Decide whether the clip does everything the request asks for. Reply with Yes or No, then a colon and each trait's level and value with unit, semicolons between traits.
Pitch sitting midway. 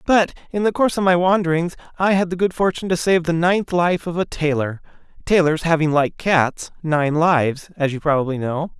Yes: medium, 165 Hz